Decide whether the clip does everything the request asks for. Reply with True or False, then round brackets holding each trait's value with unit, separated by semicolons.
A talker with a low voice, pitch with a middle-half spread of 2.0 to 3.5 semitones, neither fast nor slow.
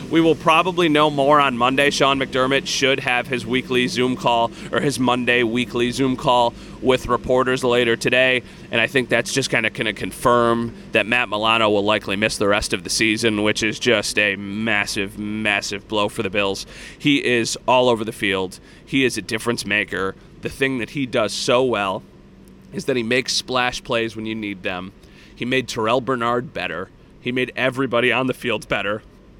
True (120 Hz; 2.9 semitones; 195 wpm)